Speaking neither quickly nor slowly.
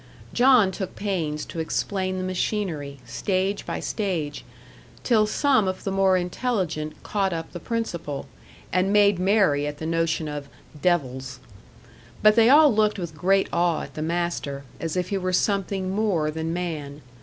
Yes: average, 160 wpm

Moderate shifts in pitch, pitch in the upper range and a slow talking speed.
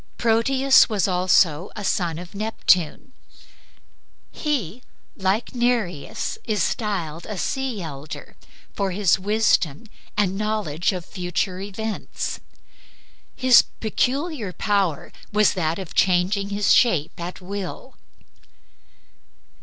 Yes: average, 3.7 semitones; high, 200 Hz; slow, 105 wpm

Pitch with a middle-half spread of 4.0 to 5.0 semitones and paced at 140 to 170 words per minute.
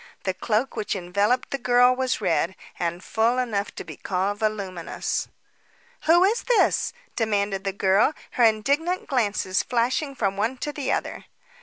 Yes: average, 4.5 semitones; average, 155 wpm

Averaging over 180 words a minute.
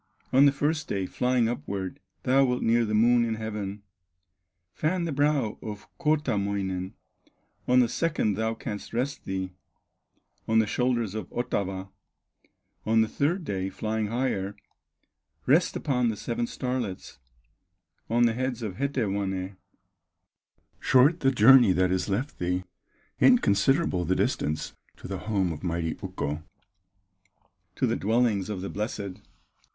No: slow, 135 wpm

